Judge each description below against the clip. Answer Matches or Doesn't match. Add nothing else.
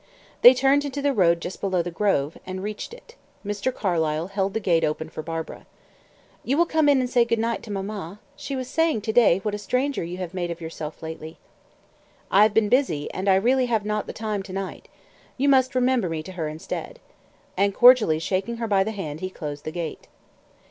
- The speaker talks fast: Matches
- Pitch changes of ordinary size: Doesn't match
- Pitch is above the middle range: Matches